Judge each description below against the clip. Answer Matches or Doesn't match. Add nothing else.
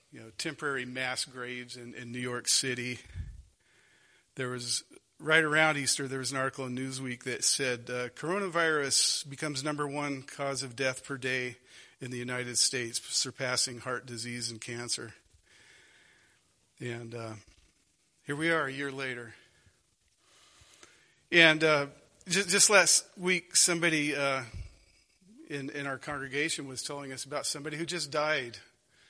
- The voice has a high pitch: Doesn't match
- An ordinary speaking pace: Matches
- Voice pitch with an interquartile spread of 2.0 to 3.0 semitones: Doesn't match